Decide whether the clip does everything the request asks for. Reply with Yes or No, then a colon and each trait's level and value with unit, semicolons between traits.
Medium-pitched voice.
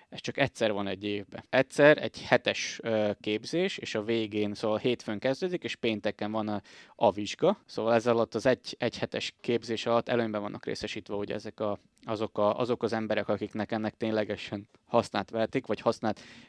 No: low, 110 Hz